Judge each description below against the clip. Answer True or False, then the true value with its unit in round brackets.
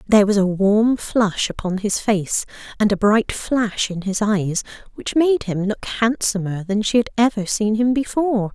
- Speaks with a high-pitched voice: True (210 Hz)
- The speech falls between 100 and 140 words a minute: False (190 wpm)